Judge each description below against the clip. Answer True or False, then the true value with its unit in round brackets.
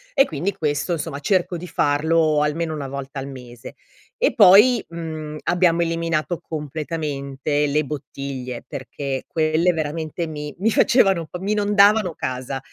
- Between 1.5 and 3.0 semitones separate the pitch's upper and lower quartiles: False (3.5 semitones)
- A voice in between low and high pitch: True (155 Hz)